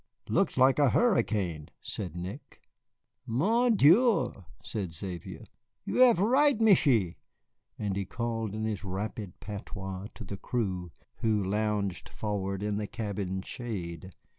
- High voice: No, low, 105 Hz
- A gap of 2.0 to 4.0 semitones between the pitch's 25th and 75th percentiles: No, average, 4.8 semitones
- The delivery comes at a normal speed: No, slow, 130 wpm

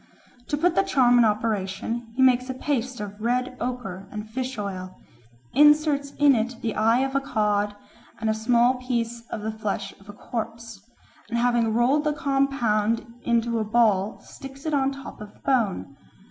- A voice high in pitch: Yes, high, 235 Hz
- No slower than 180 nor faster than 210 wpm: Yes, average, 185 wpm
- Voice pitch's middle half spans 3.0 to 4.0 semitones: Yes, average, 3.5 semitones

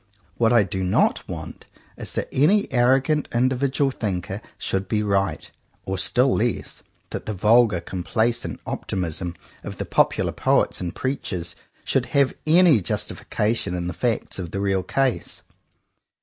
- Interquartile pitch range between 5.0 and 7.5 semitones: Yes, wide, 5.6 semitones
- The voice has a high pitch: No, low, 110 Hz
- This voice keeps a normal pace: Yes, average, 150 wpm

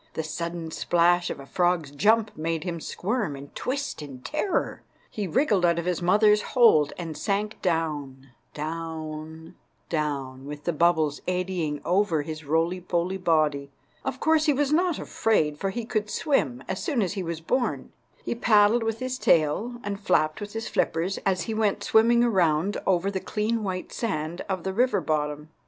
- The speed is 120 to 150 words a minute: No, average, 175 wpm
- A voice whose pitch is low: No, medium, 175 Hz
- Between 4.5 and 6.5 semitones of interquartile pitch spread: Yes, wide, 5.4 semitones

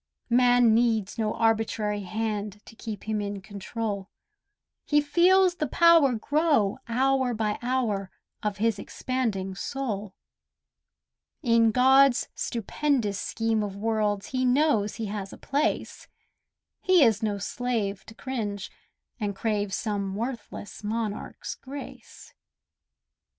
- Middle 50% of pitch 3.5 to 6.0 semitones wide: Yes, average, 3.8 semitones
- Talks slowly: Yes, slow, 120 wpm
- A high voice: Yes, high, 225 Hz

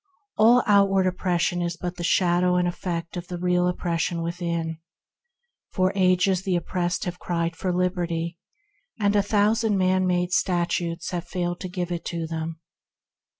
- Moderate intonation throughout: No, narrow, 1.4 semitones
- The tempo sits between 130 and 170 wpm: Yes, average, 155 wpm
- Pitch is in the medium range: Yes, medium, 180 Hz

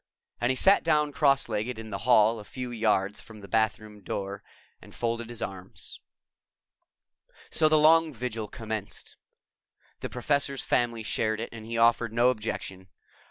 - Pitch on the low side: Yes, low, 115 Hz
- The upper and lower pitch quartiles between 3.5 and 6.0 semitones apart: No, average, 2.8 semitones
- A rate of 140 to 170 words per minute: Yes, average, 160 wpm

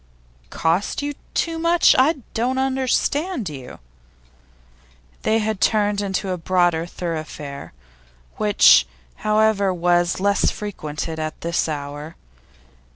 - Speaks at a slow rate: Yes, slow, 105 wpm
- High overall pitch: Yes, high, 195 Hz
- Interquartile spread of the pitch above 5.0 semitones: Yes, wide, 5.5 semitones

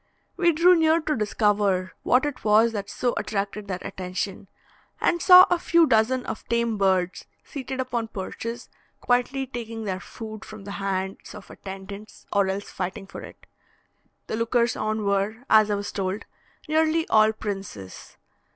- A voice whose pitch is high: Yes, high, 215 Hz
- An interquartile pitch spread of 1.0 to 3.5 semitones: No, average, 4.0 semitones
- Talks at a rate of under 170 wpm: Yes, average, 160 wpm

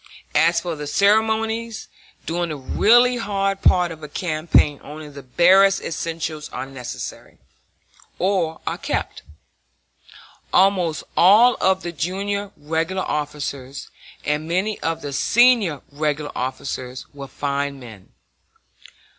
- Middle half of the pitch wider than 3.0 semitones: Yes, average, 5.1 semitones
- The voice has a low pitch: No, medium, 165 Hz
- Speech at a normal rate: No, slow, 110 wpm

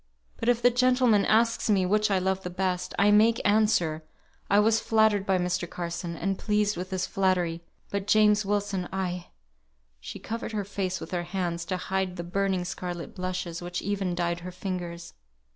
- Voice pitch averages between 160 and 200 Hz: Yes, high, 190 Hz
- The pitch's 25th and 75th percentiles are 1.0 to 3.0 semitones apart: Yes, average, 2.7 semitones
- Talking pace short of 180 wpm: No, average, 185 wpm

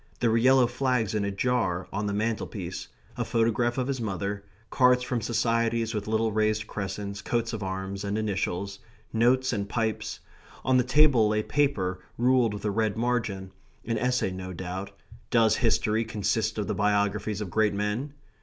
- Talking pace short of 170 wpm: No, average, 175 wpm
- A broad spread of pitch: No, average, 2.9 semitones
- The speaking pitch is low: Yes, low, 110 Hz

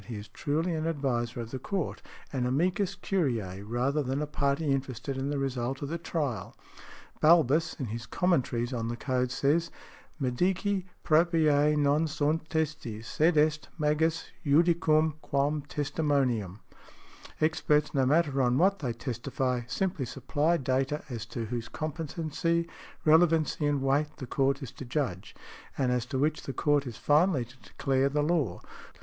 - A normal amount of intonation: Yes, average, 3.8 semitones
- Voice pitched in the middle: Yes, medium, 145 Hz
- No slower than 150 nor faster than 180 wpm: Yes, average, 155 wpm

